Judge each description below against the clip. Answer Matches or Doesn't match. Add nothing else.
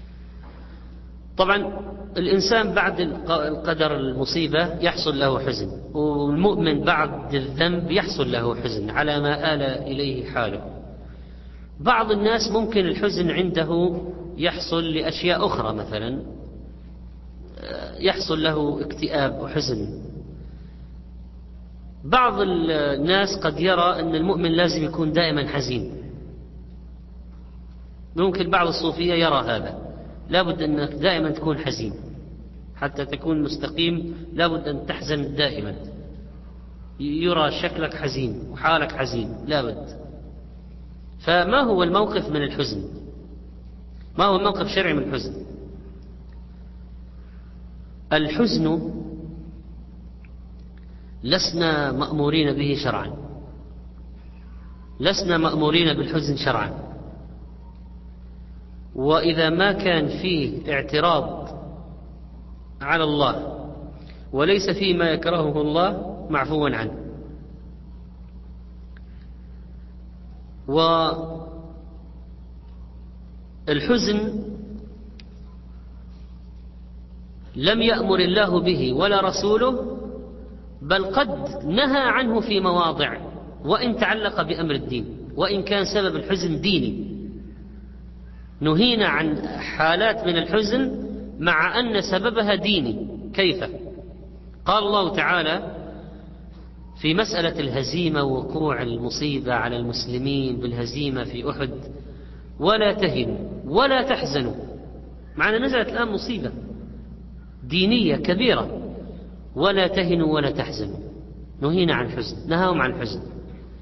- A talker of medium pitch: Matches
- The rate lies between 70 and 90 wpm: Matches